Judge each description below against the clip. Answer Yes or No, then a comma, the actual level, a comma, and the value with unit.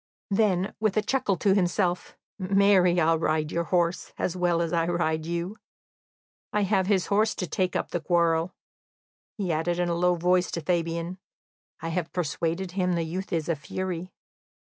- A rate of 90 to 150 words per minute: No, average, 175 wpm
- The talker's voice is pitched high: No, medium, 175 Hz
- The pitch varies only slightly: Yes, narrow, 2.0 semitones